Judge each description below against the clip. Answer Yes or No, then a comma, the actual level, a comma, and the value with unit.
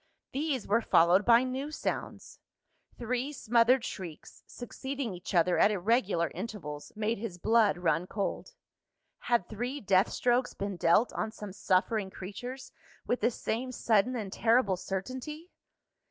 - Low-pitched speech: No, high, 220 Hz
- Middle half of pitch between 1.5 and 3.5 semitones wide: No, average, 4.8 semitones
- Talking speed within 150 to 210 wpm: No, average, 140 wpm